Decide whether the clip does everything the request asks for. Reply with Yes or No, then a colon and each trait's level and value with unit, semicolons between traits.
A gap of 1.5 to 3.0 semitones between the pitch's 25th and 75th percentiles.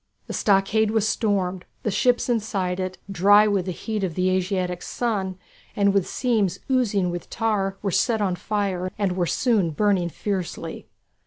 Yes: narrow, 2.5 semitones